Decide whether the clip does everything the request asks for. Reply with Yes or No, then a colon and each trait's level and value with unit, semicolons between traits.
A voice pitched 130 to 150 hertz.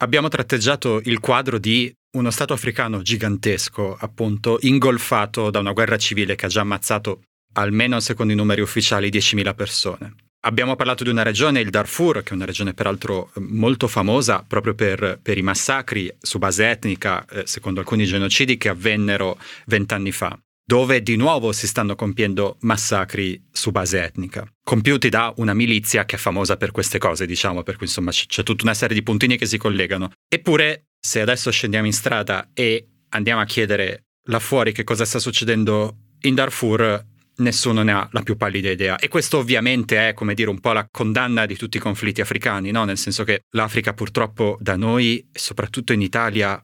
No: low, 110 Hz